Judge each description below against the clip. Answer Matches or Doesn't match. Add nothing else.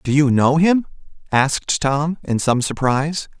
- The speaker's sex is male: Matches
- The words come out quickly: Doesn't match